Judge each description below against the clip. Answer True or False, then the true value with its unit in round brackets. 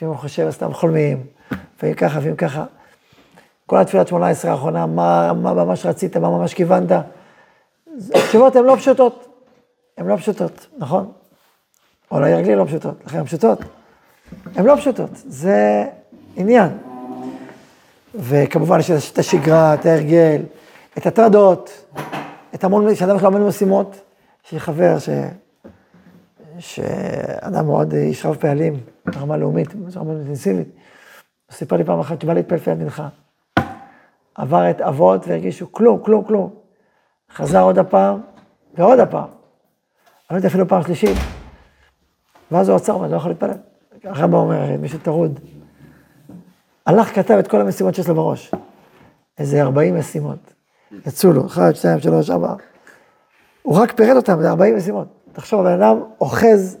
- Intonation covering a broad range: True (7.1 semitones)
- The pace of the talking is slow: False (135 wpm)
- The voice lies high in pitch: False (170 Hz)